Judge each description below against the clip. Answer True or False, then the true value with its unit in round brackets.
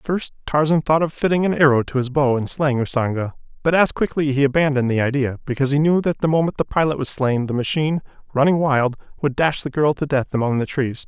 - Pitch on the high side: False (140 Hz)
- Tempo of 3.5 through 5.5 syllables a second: False (6.2 syllables/s)